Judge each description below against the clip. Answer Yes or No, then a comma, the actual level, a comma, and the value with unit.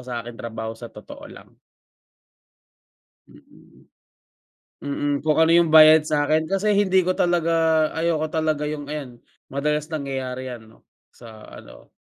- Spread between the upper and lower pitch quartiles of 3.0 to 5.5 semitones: Yes, average, 4.2 semitones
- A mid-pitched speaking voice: Yes, medium, 150 Hz